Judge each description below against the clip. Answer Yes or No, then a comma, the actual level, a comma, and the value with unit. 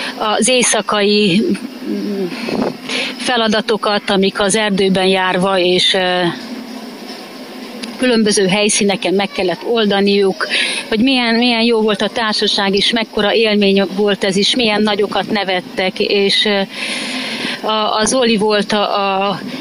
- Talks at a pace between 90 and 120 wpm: Yes, average, 110 wpm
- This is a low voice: No, high, 210 Hz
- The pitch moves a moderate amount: Yes, average, 3.0 semitones